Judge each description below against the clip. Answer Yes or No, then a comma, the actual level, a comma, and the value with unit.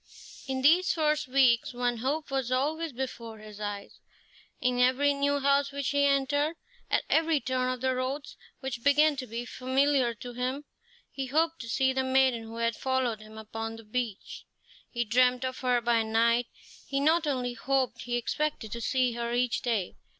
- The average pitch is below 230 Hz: No, very high, 255 Hz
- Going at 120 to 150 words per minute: No, average, 180 wpm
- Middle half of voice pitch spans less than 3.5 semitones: Yes, average, 2.9 semitones